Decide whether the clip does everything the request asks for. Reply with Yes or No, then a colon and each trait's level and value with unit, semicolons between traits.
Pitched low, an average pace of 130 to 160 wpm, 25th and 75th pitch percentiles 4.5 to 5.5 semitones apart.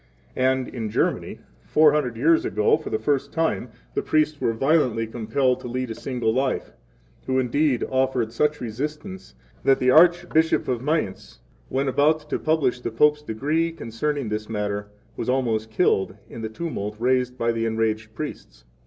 No: low, 130 Hz; average, 170 wpm; average, 5.0 semitones